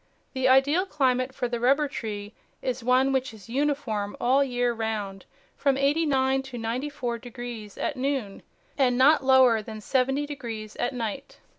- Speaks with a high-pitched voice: Yes, very high, 255 Hz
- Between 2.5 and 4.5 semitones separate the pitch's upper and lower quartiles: Yes, average, 2.9 semitones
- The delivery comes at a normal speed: Yes, average, 170 wpm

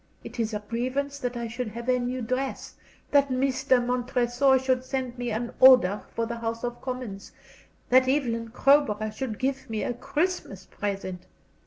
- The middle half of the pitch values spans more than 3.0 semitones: No, narrow, 2.4 semitones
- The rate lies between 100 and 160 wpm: No, average, 170 wpm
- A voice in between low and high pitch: No, high, 245 Hz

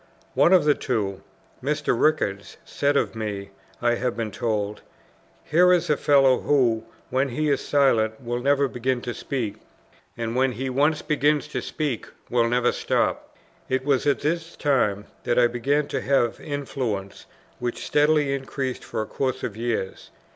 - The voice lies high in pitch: No, low, 130 Hz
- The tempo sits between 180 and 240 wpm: No, average, 165 wpm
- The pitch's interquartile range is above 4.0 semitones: No, average, 3.6 semitones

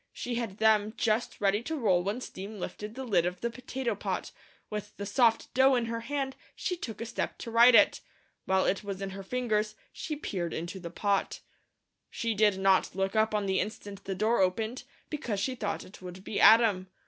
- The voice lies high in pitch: Yes, high, 215 Hz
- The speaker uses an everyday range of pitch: Yes, average, 3.4 semitones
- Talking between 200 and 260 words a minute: Yes, fast, 205 wpm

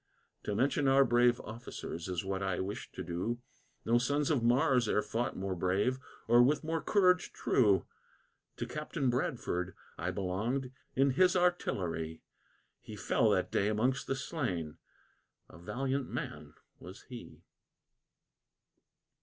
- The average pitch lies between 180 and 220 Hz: No, low, 120 Hz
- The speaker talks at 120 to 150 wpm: Yes, slow, 135 wpm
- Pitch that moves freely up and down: Yes, wide, 6.1 semitones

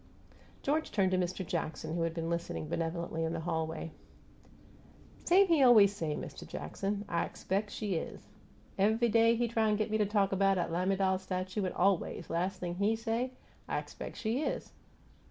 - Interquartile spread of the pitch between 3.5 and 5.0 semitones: Yes, average, 4.2 semitones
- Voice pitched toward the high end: Yes, high, 195 Hz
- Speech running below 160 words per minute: No, average, 185 wpm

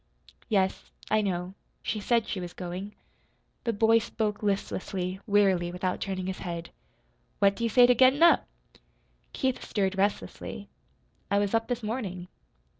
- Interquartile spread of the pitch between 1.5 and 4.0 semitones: Yes, average, 3.4 semitones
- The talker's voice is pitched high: Yes, high, 200 Hz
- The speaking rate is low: No, average, 150 wpm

